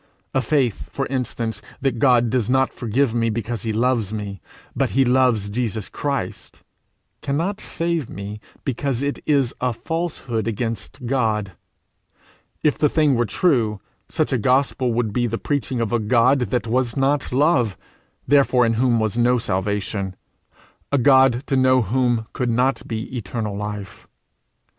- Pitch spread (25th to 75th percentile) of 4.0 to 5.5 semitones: No, average, 3.3 semitones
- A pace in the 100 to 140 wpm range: No, average, 155 wpm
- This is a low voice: Yes, low, 120 Hz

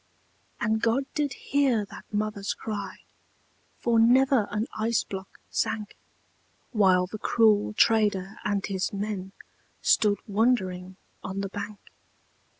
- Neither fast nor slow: No, slow, 120 wpm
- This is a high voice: Yes, high, 210 Hz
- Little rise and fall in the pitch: Yes, narrow, 2.3 semitones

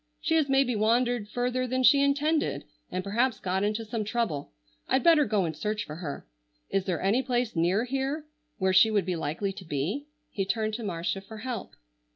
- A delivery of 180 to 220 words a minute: Yes, average, 200 wpm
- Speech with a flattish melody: No, average, 5.1 semitones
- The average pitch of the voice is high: Yes, high, 215 Hz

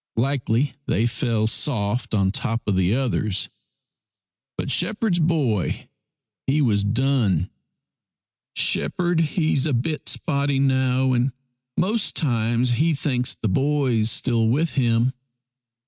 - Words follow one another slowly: Yes, slow, 120 wpm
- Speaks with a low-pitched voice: Yes, low, 125 Hz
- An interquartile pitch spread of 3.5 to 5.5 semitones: Yes, average, 4.2 semitones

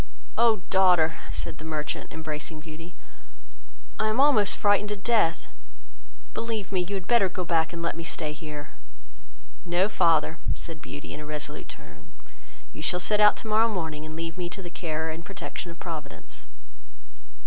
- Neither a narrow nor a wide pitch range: Yes, average, 4.0 semitones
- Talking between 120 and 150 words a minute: No, average, 170 wpm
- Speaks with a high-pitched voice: No, medium, 170 Hz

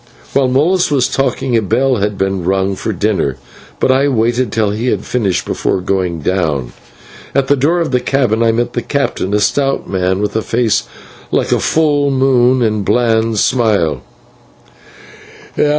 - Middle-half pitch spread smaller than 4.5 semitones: No, average, 5.1 semitones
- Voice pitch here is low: Yes, low, 115 Hz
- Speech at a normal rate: Yes, average, 165 wpm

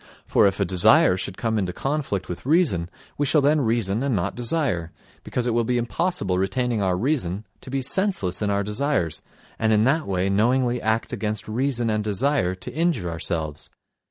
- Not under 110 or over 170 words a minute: No, average, 185 wpm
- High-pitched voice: No, low, 110 Hz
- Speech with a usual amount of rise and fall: No, wide, 5.9 semitones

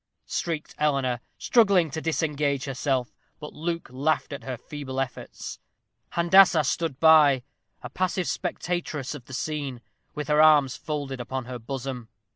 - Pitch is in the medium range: Yes, medium, 145 Hz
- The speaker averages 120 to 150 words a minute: Yes, average, 140 wpm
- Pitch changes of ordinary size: Yes, average, 3.2 semitones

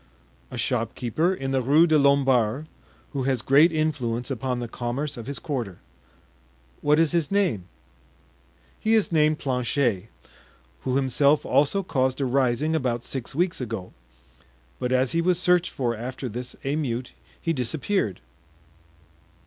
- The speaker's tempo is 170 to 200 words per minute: No, average, 140 wpm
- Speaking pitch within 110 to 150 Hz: Yes, low, 135 Hz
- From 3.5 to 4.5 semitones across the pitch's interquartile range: Yes, average, 4.1 semitones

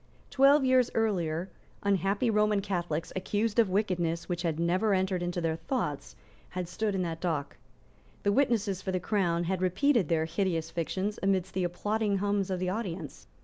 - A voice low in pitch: No, high, 190 Hz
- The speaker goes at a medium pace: Yes, average, 170 wpm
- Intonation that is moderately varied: Yes, average, 3.4 semitones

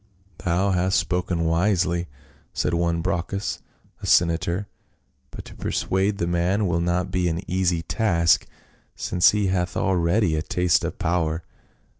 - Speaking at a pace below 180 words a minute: Yes, average, 150 wpm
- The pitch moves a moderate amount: No, narrow, 1.9 semitones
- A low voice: Yes, very low, 90 Hz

